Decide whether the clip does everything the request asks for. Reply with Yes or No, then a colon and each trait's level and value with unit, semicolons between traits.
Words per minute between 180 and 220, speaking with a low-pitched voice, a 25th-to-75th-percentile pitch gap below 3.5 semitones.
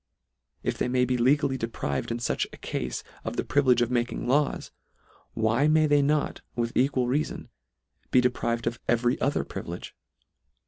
No: average, 165 wpm; low, 125 Hz; average, 3.1 semitones